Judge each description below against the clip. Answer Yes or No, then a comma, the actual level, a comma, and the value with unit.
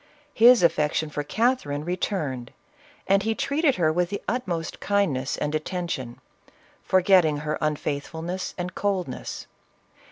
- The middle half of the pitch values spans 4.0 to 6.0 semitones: Yes, average, 4.8 semitones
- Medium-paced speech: No, slow, 120 wpm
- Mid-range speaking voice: Yes, medium, 175 Hz